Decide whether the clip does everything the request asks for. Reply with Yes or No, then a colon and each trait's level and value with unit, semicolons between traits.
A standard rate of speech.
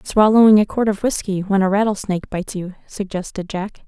Yes: average, 185 wpm